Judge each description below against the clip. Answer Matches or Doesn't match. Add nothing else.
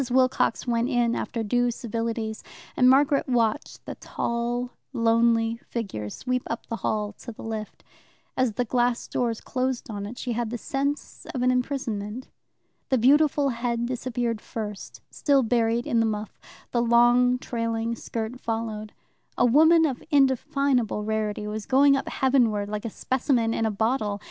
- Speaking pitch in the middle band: Doesn't match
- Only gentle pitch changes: Matches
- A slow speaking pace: Doesn't match